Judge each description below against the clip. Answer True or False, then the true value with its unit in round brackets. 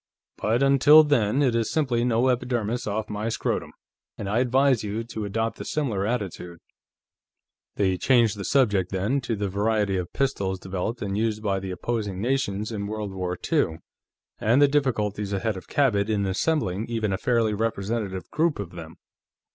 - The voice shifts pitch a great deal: False (3.8 semitones)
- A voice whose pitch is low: True (110 Hz)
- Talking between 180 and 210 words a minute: False (170 wpm)